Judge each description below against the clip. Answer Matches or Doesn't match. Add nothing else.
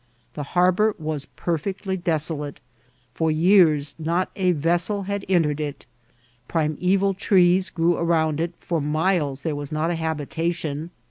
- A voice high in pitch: Doesn't match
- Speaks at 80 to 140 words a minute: Matches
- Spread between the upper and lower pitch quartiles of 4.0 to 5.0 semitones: Doesn't match